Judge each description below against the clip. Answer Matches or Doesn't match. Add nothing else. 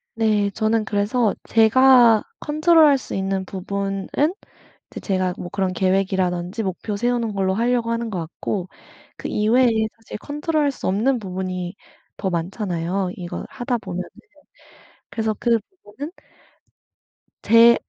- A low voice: Doesn't match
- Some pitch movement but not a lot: Matches